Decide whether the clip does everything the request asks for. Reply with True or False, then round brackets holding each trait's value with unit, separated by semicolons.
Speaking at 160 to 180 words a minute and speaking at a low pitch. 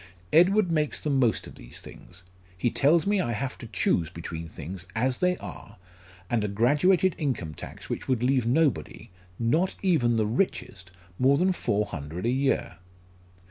True (170 wpm; 125 Hz)